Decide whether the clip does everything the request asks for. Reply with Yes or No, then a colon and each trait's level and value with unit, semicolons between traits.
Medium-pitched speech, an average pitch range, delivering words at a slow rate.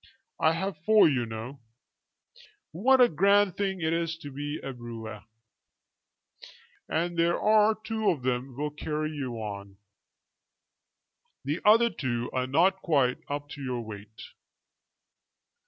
No: medium, 150 Hz; wide, 7.0 semitones; slow, 130 wpm